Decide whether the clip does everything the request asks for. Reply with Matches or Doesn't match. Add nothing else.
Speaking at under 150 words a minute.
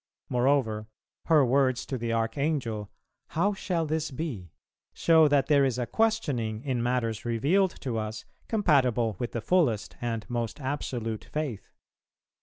Matches